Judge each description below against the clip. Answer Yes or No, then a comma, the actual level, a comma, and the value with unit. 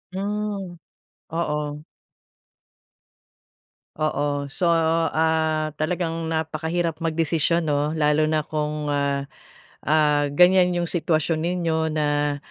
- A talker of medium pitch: Yes, medium, 160 Hz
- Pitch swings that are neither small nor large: No, narrow, 2.0 semitones